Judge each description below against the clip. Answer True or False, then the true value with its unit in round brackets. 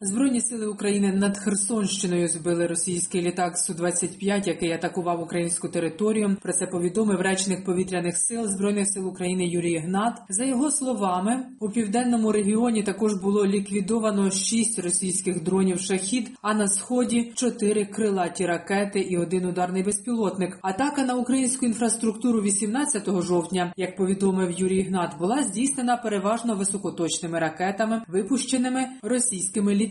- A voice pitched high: True (200 Hz)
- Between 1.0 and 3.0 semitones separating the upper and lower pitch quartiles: False (3.8 semitones)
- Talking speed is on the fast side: False (130 wpm)